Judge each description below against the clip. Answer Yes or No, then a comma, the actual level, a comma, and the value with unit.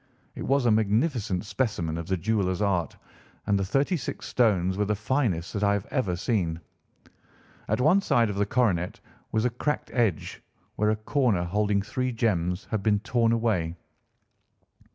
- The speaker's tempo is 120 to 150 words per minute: No, average, 170 wpm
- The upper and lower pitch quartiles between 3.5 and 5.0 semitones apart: Yes, average, 4.3 semitones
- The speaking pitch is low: Yes, low, 105 Hz